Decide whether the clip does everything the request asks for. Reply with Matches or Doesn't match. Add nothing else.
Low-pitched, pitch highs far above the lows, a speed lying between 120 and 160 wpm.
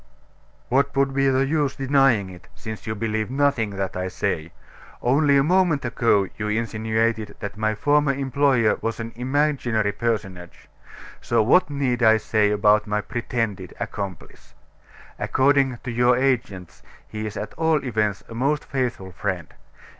Doesn't match